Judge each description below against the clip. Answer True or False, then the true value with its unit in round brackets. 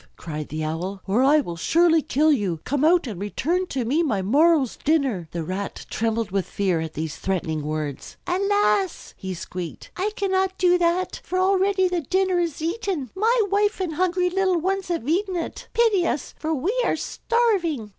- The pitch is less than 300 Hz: False (315 Hz)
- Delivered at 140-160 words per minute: False (185 wpm)